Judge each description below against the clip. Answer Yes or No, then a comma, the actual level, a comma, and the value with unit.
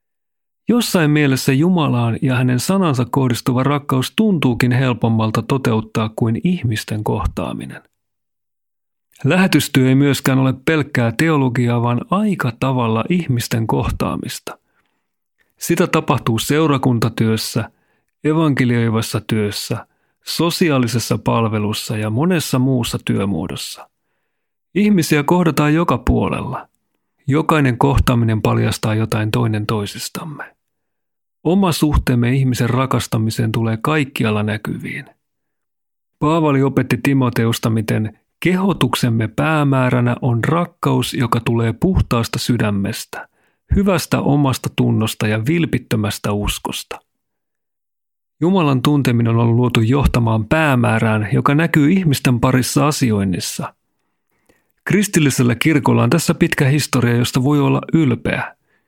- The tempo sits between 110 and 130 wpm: No, slow, 95 wpm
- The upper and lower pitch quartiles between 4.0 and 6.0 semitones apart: Yes, average, 4.4 semitones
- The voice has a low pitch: Yes, low, 130 Hz